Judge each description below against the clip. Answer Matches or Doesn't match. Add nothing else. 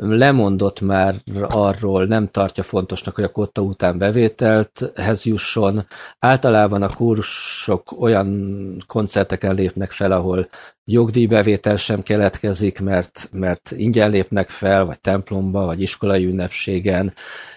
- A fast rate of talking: Doesn't match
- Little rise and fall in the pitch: Matches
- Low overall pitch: Matches